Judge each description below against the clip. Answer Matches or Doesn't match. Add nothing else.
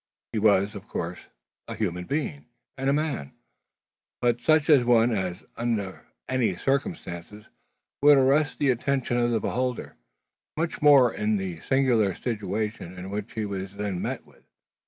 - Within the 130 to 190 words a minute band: Matches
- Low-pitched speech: Matches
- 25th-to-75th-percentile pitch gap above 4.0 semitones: Matches